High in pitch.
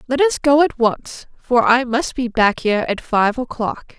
Yes: very high, 250 Hz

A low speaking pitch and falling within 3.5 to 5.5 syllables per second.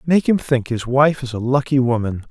Yes: low, 130 Hz; 5.1 syllables/s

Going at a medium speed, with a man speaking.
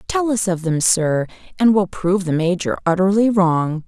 No: average, 185 wpm; female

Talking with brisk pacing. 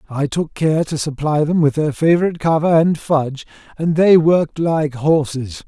No: average, 180 wpm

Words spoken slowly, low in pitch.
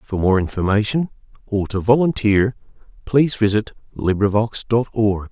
Yes: slow, 125 wpm; low, 110 Hz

